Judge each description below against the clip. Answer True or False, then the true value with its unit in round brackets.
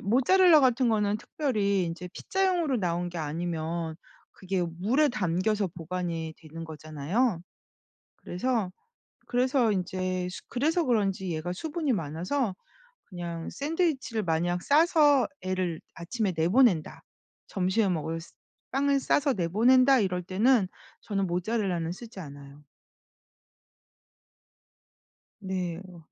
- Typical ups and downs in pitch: False (6.7 semitones)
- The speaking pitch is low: False (190 Hz)